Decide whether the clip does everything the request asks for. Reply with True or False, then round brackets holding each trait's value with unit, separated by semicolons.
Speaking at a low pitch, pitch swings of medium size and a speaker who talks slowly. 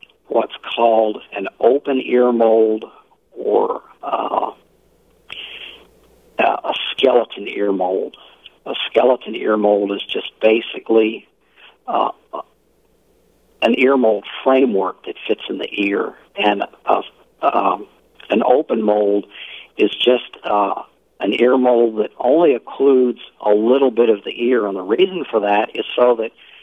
True (115 Hz; 4.1 semitones; 130 wpm)